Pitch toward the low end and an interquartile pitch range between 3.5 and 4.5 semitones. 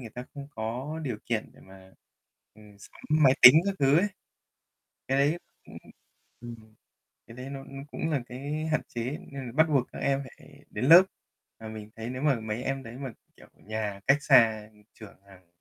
Yes: low, 125 Hz; average, 4.2 semitones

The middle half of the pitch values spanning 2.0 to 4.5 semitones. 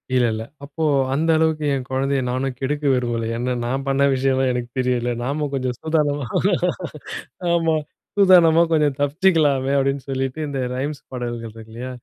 Yes: average, 2.8 semitones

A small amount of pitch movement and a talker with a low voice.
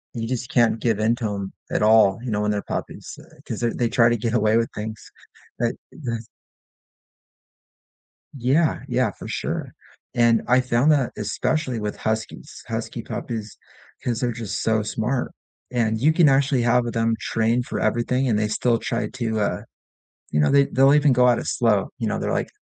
Yes: narrow, 2.3 semitones; low, 115 Hz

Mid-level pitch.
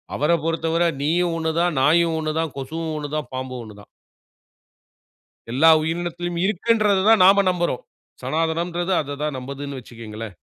Yes: medium, 160 Hz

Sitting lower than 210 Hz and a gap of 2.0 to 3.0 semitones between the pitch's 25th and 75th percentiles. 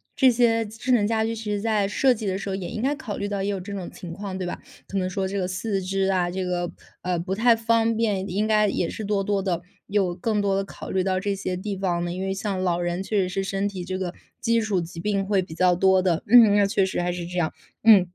Yes: high, 195 Hz; narrow, 2.4 semitones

